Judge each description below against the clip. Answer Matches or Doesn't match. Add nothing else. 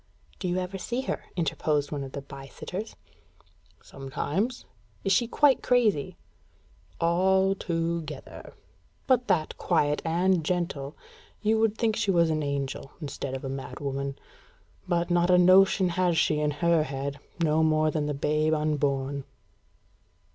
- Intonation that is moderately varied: Matches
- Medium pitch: Matches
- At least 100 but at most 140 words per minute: Doesn't match